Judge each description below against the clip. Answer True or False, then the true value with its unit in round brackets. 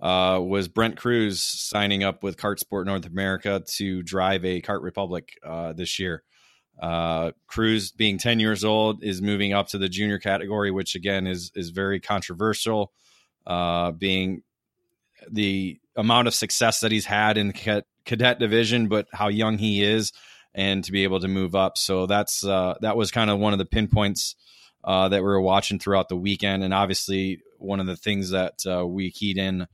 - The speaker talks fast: False (190 wpm)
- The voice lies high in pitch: False (100 Hz)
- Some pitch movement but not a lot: False (1.9 semitones)